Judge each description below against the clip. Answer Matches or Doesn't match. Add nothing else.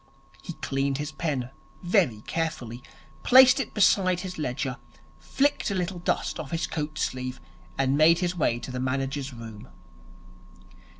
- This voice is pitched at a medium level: Matches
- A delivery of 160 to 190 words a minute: Doesn't match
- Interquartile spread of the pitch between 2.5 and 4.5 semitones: Doesn't match